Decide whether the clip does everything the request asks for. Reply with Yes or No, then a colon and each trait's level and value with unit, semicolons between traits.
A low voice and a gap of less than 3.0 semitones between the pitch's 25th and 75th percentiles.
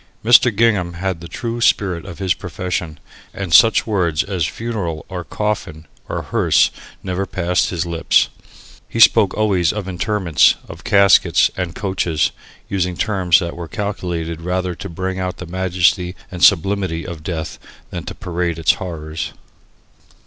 Yes: very low, 90 Hz; narrow, 2.6 semitones